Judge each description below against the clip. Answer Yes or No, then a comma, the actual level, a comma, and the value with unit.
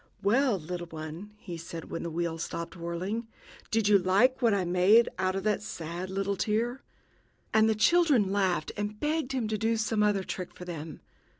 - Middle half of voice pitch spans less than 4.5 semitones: Yes, average, 4.1 semitones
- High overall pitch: Yes, high, 200 Hz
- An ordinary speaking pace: Yes, average, 190 wpm